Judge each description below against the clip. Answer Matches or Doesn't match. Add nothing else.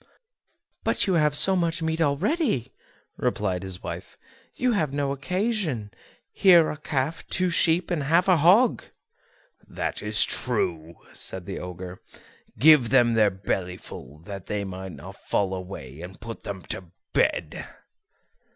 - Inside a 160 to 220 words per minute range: Doesn't match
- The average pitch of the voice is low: Matches